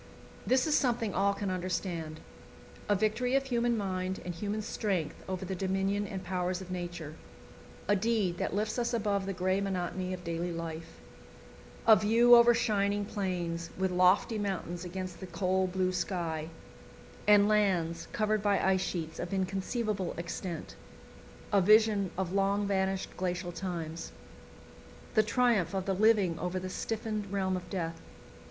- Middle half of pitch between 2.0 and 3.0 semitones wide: Yes, narrow, 2.6 semitones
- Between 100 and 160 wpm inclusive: Yes, average, 155 wpm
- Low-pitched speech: No, high, 190 Hz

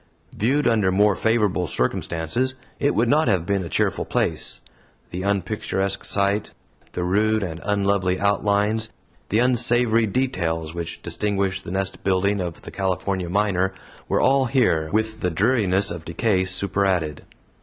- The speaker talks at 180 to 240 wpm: No, average, 145 wpm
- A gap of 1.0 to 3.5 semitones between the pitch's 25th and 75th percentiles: Yes, average, 3.1 semitones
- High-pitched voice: No, low, 100 Hz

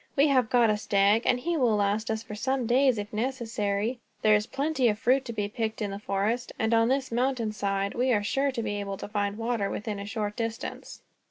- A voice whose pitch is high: Yes, high, 225 Hz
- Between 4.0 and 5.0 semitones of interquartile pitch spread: No, average, 3.2 semitones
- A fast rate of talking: Yes, fast, 235 wpm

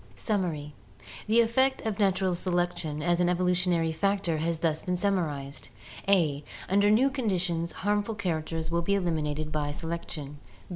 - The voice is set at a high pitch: No, medium, 175 Hz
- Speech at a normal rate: Yes, average, 145 wpm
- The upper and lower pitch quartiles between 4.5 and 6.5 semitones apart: No, average, 3.9 semitones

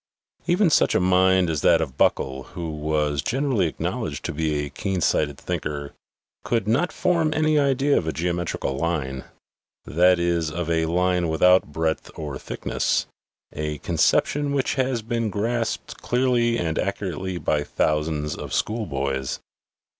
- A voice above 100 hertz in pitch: No, very low, 85 Hz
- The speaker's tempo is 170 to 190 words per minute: No, average, 150 wpm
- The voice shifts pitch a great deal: Yes, wide, 7.4 semitones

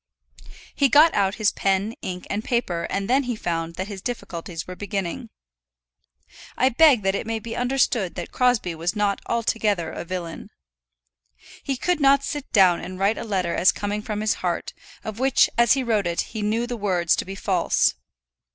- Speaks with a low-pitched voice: No, high, 210 Hz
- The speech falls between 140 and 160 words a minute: No, average, 190 wpm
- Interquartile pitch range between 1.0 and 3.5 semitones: No, average, 4.5 semitones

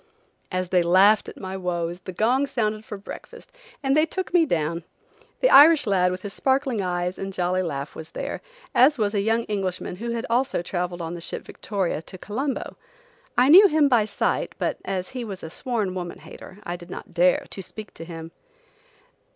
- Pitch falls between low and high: No, high, 195 Hz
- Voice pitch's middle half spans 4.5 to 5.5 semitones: Yes, average, 5.2 semitones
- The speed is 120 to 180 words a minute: No, average, 200 wpm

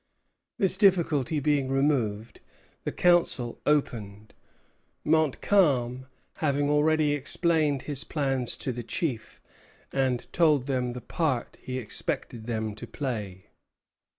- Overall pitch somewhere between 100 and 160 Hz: Yes, low, 135 Hz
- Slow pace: Yes, slow, 110 wpm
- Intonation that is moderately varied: Yes, average, 4.0 semitones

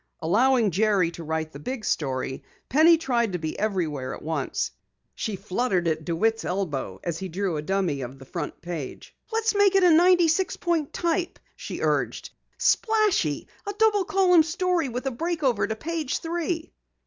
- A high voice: Yes, high, 225 Hz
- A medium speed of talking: Yes, average, 170 wpm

